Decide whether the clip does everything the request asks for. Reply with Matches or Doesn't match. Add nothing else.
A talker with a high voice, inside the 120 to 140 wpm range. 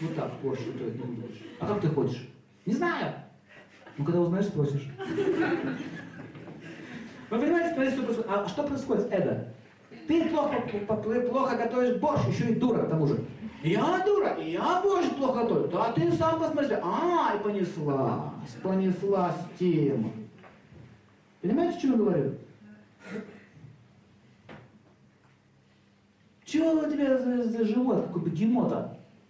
Matches